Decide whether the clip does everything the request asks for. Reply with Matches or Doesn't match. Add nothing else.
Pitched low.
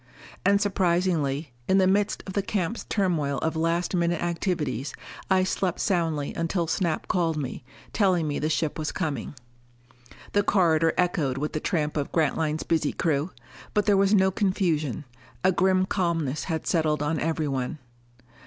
Doesn't match